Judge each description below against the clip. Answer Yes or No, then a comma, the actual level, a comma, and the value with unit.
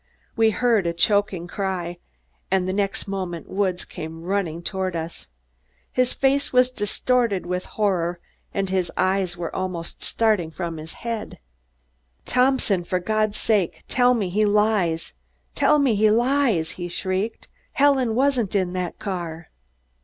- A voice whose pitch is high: Yes, high, 195 Hz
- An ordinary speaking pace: Yes, average, 145 wpm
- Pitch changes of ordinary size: Yes, average, 4.1 semitones